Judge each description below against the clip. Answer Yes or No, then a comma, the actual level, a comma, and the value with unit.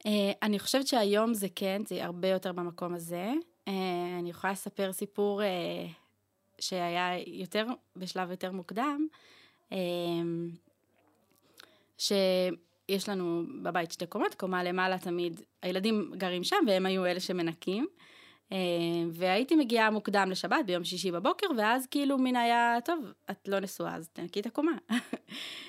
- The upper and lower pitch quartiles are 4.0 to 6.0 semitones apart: No, average, 3.6 semitones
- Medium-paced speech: Yes, average, 140 wpm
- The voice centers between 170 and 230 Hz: Yes, high, 190 Hz